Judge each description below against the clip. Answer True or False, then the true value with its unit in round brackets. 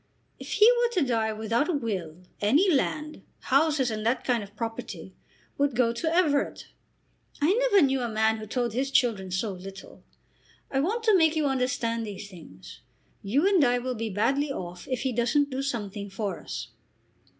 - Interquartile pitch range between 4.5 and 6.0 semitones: True (5.2 semitones)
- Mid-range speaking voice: False (245 Hz)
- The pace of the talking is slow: False (185 wpm)